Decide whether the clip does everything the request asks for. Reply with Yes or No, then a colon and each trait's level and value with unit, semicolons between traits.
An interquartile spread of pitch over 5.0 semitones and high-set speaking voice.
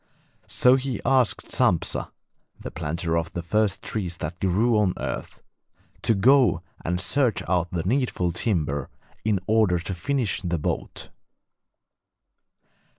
No: wide, 5.4 semitones; very low, 95 Hz